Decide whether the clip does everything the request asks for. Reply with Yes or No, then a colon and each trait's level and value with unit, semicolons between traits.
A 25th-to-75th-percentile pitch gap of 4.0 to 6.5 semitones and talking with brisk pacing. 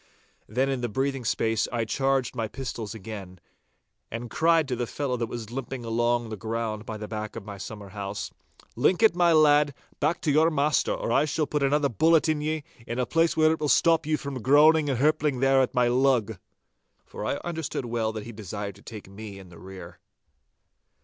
Yes: average, 5.1 semitones; fast, 210 wpm